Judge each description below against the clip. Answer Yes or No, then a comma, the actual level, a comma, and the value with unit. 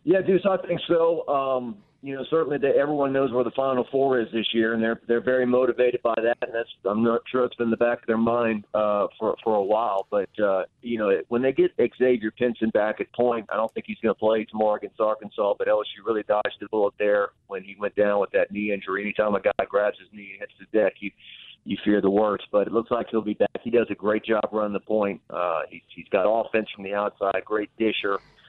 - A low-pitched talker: Yes, low, 115 Hz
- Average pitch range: Yes, average, 4.1 semitones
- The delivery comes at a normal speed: No, fast, 255 wpm